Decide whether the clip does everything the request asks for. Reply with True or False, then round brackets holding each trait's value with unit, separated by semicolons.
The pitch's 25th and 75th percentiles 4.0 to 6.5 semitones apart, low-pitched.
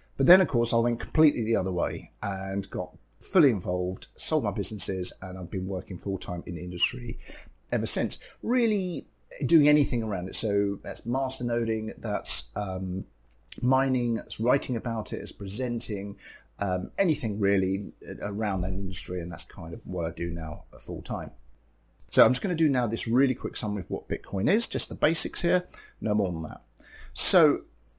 True (4.7 semitones; 100 Hz)